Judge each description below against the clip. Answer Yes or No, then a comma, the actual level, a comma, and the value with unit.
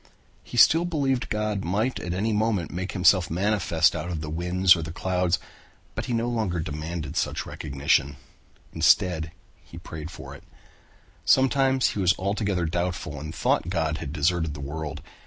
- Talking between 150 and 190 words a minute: Yes, average, 170 wpm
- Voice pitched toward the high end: No, very low, 90 Hz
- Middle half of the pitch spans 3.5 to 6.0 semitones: Yes, average, 4.7 semitones